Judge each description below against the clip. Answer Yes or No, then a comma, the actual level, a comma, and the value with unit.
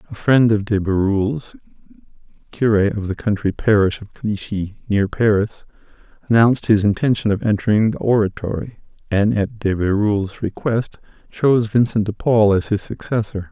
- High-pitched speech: No, low, 105 Hz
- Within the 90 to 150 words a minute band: Yes, average, 145 wpm